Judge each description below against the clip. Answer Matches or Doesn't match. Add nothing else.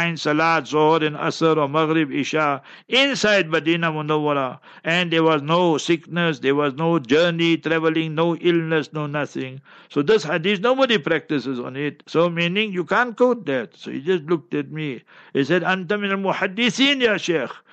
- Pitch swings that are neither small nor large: Matches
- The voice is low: Doesn't match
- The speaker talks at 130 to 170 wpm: Matches